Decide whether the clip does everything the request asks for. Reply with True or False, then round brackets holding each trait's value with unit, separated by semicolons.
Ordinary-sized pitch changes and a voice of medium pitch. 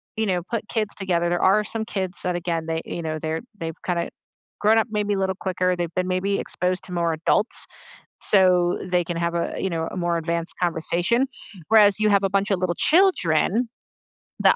True (3.1 semitones; 180 Hz)